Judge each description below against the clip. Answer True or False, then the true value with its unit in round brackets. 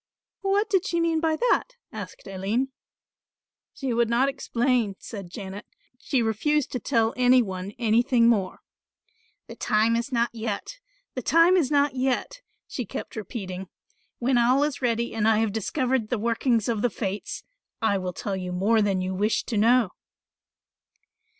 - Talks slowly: False (165 wpm)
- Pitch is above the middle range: True (235 Hz)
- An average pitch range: True (4.1 semitones)